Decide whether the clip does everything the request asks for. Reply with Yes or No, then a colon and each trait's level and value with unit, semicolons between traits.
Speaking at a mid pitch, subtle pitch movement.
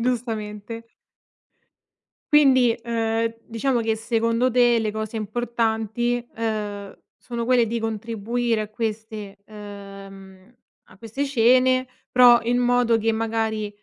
No: high, 225 Hz; narrow, 2.0 semitones